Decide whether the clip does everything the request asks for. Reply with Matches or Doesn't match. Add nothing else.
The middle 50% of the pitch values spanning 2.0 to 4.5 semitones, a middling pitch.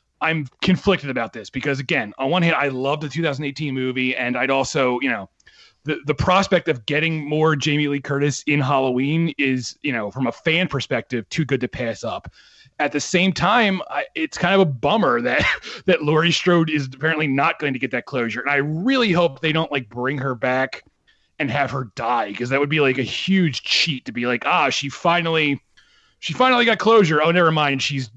Matches